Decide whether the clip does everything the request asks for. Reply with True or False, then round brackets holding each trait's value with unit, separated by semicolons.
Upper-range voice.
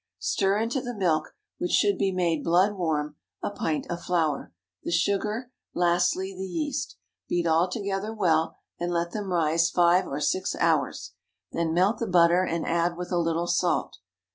False (175 Hz)